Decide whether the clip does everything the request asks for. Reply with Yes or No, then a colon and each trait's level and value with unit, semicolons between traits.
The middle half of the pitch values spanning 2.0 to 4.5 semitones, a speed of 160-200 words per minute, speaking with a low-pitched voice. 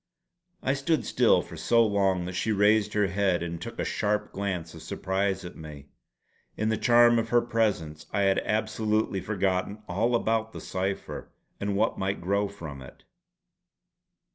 Yes: average, 3.0 semitones; average, 165 wpm; low, 100 Hz